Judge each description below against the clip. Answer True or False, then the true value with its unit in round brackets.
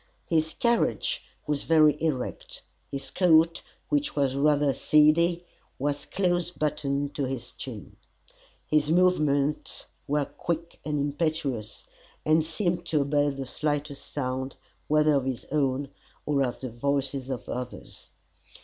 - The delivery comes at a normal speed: False (130 wpm)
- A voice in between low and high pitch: True (150 Hz)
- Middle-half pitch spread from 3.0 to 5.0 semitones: False (2.6 semitones)